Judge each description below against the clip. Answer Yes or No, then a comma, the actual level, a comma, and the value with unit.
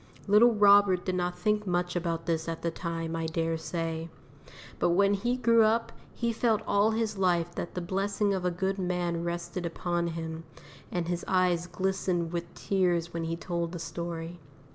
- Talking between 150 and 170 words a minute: No, average, 185 wpm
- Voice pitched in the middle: Yes, medium, 175 Hz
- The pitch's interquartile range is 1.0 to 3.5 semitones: Yes, narrow, 2.6 semitones